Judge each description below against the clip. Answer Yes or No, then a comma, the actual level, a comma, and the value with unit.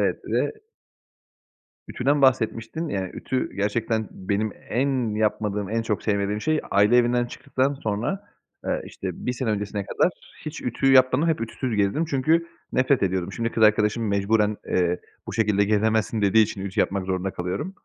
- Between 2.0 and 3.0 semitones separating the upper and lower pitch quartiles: No, average, 4.2 semitones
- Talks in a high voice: No, low, 110 Hz